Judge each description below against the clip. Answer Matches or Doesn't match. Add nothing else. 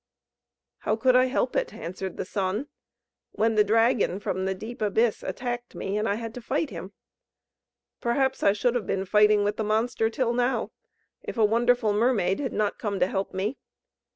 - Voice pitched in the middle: Doesn't match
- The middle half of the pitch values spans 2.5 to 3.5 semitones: Matches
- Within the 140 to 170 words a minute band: Doesn't match